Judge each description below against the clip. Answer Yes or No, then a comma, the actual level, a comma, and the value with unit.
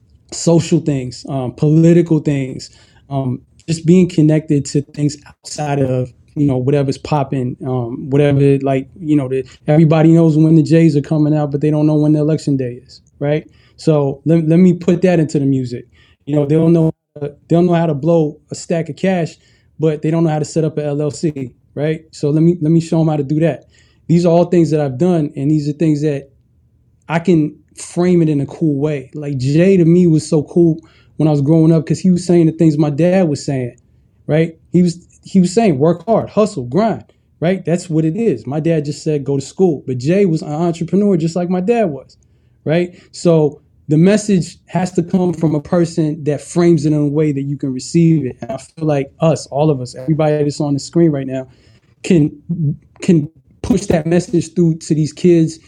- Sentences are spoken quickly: Yes, fast, 220 wpm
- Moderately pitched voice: Yes, medium, 155 Hz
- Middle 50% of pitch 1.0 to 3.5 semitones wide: Yes, average, 2.8 semitones